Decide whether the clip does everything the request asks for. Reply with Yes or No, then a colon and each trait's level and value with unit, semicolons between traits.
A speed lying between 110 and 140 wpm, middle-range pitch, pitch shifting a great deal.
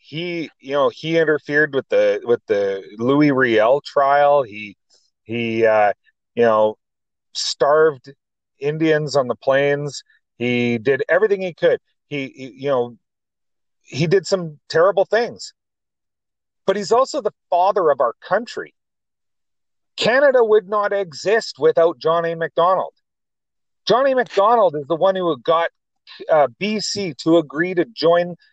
Yes: slow, 135 wpm; medium, 160 Hz; wide, 6.1 semitones